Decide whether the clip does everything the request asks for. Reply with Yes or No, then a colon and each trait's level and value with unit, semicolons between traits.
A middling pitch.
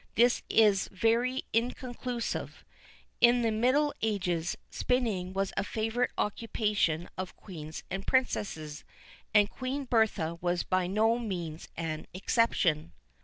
No: high, 210 Hz